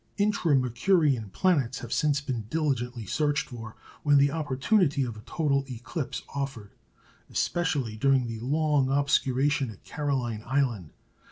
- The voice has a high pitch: No, low, 135 Hz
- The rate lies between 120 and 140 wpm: Yes, slow, 135 wpm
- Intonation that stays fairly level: No, average, 3.7 semitones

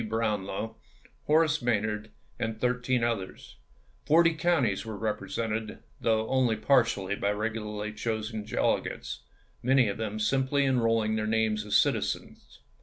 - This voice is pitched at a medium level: No, low, 110 Hz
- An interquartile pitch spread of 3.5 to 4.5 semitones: No, narrow, 2.6 semitones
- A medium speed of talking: No, slow, 125 wpm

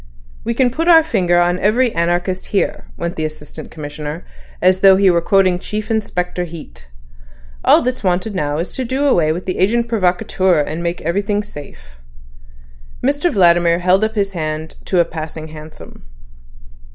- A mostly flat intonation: No, average, 4.3 semitones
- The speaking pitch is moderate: Yes, medium, 180 Hz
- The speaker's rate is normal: Yes, average, 170 wpm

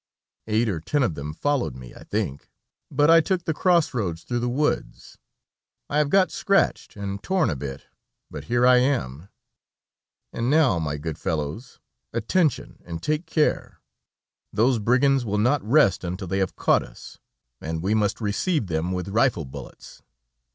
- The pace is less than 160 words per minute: No, average, 165 wpm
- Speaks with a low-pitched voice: Yes, low, 110 Hz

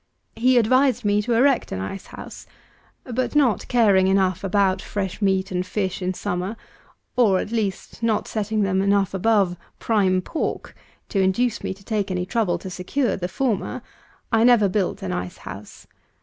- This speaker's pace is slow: No, average, 170 wpm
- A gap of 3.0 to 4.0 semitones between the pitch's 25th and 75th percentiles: Yes, average, 3.4 semitones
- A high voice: Yes, high, 200 Hz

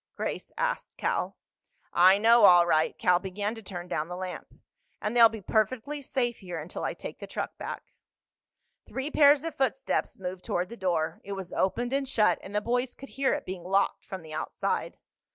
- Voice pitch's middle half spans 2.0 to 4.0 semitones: No, wide, 5.5 semitones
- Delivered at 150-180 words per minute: No, average, 195 wpm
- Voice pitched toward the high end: Yes, high, 205 Hz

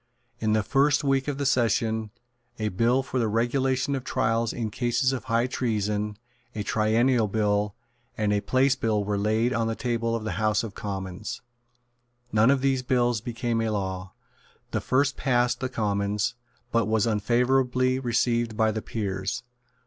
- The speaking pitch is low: Yes, low, 115 Hz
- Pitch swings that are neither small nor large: Yes, average, 3.1 semitones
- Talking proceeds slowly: No, average, 165 wpm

